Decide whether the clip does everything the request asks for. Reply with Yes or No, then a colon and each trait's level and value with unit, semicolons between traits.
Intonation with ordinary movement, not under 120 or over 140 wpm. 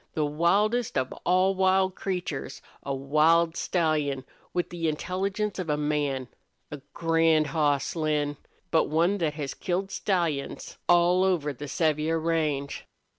Yes: average, 3.5 semitones; slow, 135 wpm